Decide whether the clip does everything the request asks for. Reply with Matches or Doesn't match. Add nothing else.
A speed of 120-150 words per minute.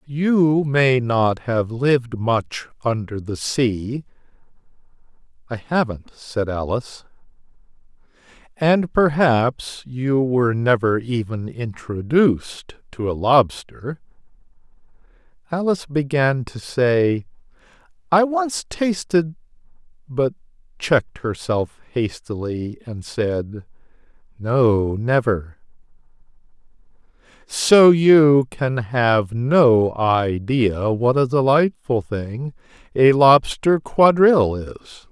Doesn't match